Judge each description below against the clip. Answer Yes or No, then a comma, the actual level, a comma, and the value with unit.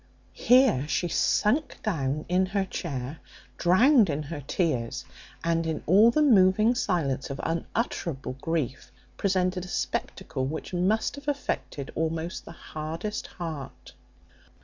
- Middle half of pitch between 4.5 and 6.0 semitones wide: Yes, average, 5.1 semitones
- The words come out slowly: Yes, slow, 125 wpm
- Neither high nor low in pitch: Yes, medium, 170 Hz